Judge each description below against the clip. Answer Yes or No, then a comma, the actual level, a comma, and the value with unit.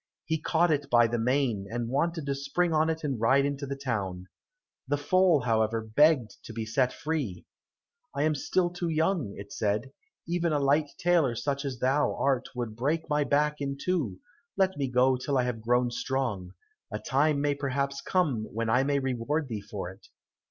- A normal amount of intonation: Yes, average, 4.4 semitones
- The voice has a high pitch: No, low, 135 Hz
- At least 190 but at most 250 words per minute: Yes, average, 195 wpm